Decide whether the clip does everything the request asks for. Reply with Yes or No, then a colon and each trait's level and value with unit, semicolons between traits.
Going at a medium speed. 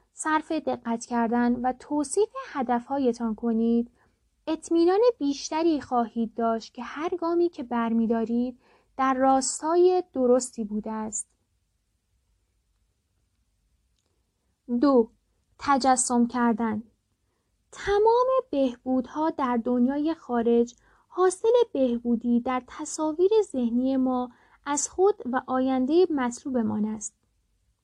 No: slow, 90 wpm